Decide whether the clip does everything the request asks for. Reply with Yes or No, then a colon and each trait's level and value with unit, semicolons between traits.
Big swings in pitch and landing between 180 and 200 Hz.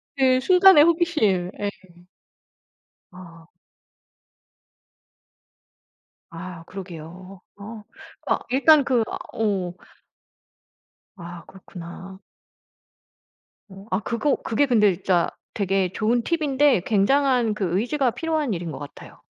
No: wide, 6.6 semitones; high, 210 Hz